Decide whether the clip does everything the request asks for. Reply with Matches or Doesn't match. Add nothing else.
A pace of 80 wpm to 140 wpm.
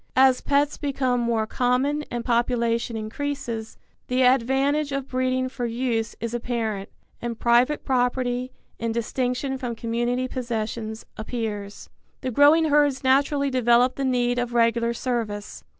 Matches